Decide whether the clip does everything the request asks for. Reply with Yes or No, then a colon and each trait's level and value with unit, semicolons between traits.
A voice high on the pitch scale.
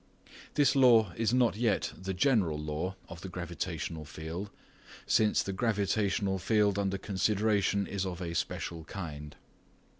No: very low, 95 Hz